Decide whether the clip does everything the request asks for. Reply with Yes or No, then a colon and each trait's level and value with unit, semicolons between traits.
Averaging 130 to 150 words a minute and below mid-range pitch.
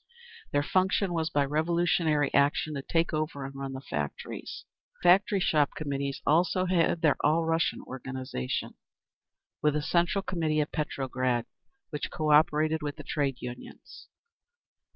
No: average, 145 wpm; medium, 150 Hz